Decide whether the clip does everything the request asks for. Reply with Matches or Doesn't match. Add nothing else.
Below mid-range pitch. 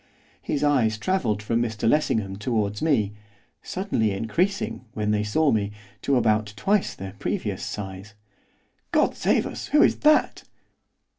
Matches